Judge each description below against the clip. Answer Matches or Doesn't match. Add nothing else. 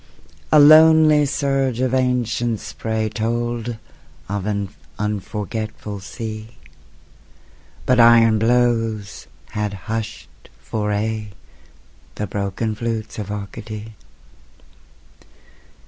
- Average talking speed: Doesn't match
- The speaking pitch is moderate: Doesn't match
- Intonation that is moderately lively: Doesn't match